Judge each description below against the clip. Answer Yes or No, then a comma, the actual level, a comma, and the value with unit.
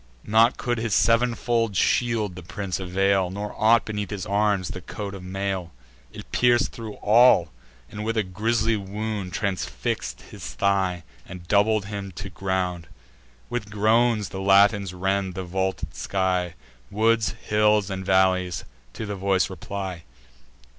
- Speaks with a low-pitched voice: Yes, low, 100 Hz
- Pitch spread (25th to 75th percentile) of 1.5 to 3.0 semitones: Yes, narrow, 2.5 semitones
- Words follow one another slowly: No, average, 145 wpm